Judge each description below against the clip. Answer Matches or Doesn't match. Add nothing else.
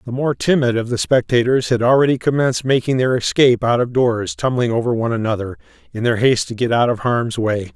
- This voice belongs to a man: Matches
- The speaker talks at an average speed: Doesn't match